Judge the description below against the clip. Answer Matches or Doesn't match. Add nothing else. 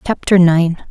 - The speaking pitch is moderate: Matches